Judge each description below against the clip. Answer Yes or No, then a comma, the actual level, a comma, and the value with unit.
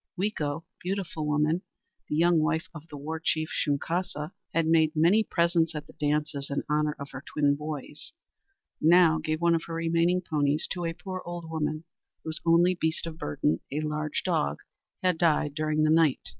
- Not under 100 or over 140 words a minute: No, average, 185 wpm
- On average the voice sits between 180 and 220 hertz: No, medium, 160 Hz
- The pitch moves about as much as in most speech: No, narrow, 2.0 semitones